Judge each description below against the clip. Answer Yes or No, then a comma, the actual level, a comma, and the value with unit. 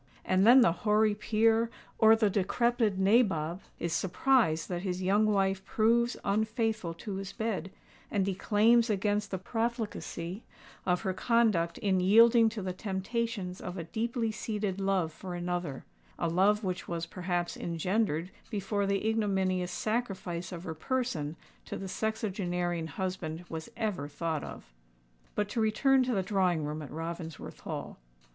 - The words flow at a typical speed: Yes, average, 150 wpm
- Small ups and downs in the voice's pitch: No, average, 3.8 semitones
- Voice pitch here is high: Yes, high, 195 Hz